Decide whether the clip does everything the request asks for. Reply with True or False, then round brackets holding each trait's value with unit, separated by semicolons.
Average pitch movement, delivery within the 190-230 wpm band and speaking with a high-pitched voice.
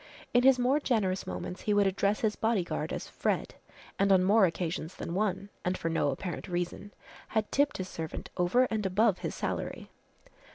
False (3.4 semitones; 180 wpm; 195 Hz)